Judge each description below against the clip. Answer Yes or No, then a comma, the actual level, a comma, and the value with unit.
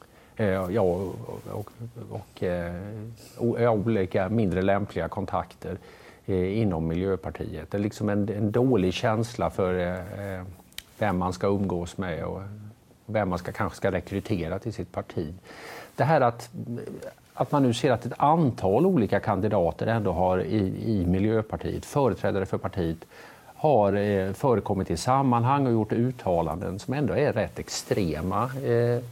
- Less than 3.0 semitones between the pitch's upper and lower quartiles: No, average, 3.5 semitones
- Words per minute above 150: No, average, 140 wpm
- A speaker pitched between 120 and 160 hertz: No, low, 100 Hz